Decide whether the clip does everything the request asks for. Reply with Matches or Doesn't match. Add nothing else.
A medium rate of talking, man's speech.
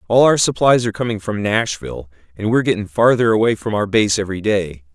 Doesn't match